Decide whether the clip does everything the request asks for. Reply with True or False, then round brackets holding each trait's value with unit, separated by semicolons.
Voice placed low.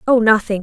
False (220 Hz)